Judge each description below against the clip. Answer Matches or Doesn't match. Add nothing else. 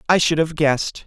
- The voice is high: Doesn't match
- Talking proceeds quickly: Matches